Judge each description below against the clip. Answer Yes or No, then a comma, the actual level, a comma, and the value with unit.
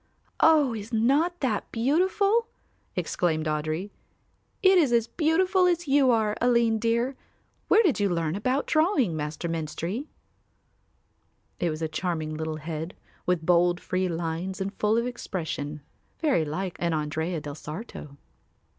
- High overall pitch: Yes, high, 195 Hz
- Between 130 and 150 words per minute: Yes, average, 140 wpm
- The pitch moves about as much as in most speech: No, wide, 8.6 semitones